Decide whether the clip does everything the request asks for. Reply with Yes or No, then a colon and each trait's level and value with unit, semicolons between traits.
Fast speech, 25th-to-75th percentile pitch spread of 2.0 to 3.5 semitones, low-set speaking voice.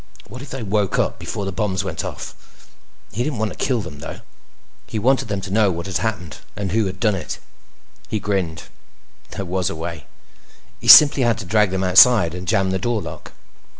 Yes: fast, 210 wpm; average, 3.2 semitones; low, 100 Hz